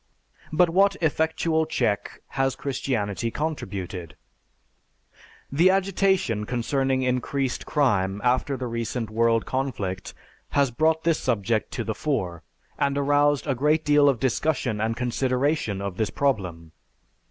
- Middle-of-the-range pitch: No, low, 130 Hz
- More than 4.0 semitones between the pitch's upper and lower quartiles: Yes, average, 5.0 semitones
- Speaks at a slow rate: Yes, slow, 125 wpm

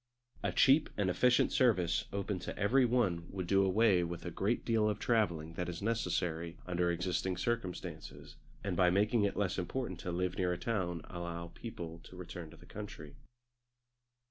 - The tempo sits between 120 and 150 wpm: No, average, 175 wpm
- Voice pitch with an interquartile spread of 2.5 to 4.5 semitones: Yes, average, 3.7 semitones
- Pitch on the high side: No, very low, 90 Hz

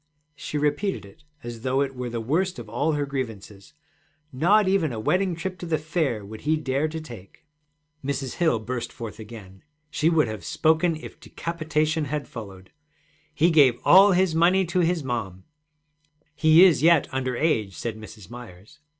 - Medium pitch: Yes, medium, 145 Hz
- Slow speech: No, average, 175 wpm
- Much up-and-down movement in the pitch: Yes, wide, 5.9 semitones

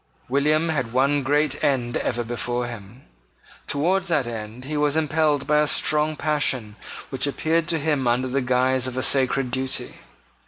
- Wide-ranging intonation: No, average, 3.3 semitones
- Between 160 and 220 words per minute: Yes, average, 165 wpm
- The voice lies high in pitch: No, low, 135 Hz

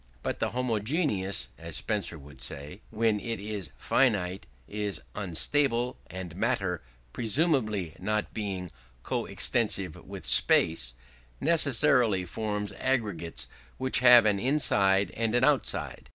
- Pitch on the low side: Yes, low, 105 Hz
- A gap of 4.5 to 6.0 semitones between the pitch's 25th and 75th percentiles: Yes, average, 4.9 semitones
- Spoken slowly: Yes, slow, 120 wpm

